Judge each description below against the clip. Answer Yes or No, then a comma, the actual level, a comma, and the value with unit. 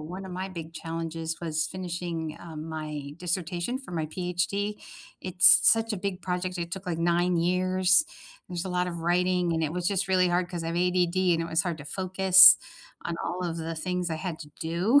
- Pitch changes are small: Yes, narrow, 1.9 semitones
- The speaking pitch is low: No, medium, 175 Hz